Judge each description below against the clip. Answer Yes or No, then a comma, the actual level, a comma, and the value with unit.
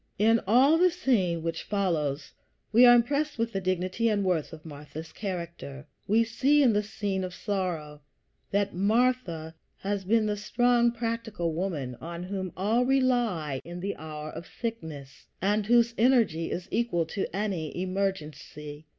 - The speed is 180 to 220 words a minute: No, average, 155 wpm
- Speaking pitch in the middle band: No, high, 195 Hz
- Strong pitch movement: Yes, wide, 5.7 semitones